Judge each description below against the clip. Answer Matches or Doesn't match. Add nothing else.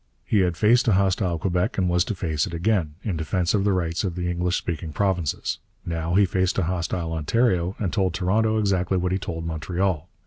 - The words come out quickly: Matches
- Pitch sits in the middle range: Doesn't match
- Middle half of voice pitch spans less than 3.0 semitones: Matches